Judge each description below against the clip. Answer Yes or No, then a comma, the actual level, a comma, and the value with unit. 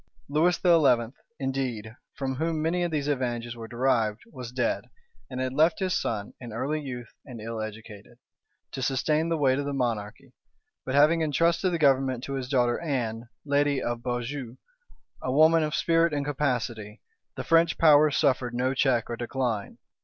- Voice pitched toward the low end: Yes, low, 130 Hz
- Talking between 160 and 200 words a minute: Yes, average, 170 wpm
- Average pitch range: Yes, average, 4.1 semitones